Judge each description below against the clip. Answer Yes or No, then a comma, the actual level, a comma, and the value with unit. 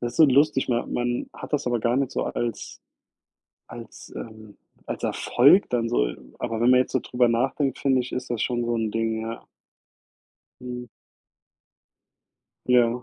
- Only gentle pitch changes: Yes, narrow, 1.6 semitones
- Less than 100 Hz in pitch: No, low, 120 Hz